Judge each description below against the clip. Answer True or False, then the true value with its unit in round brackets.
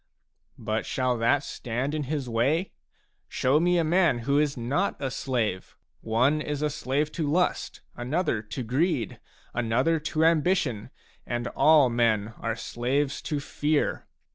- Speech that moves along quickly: False (145 wpm)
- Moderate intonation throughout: True (4.4 semitones)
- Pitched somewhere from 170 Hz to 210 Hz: False (140 Hz)